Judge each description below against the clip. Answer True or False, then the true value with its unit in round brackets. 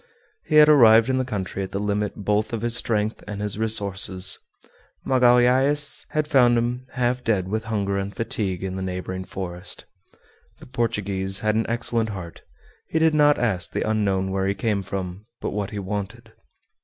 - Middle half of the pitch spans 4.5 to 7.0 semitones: False (3.7 semitones)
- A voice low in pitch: True (105 Hz)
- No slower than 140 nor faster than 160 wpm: False (180 wpm)